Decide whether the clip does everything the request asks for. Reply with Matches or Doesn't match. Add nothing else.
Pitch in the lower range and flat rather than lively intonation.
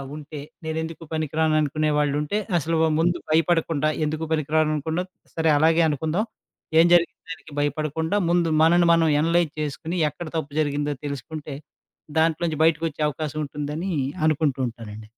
Doesn't match